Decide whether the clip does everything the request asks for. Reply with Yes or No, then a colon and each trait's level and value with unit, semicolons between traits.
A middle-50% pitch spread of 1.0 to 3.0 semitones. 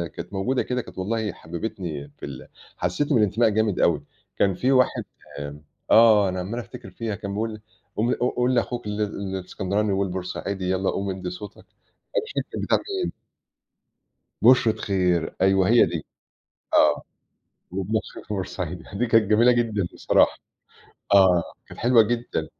No: average, 3.6 semitones